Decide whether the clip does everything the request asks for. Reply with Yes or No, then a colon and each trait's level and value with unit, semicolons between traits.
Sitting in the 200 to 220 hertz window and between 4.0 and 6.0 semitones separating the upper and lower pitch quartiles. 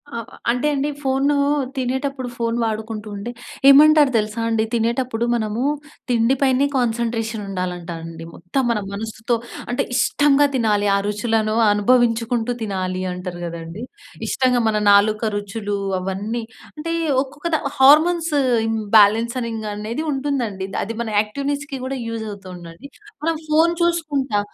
No: high, 230 Hz; average, 4.5 semitones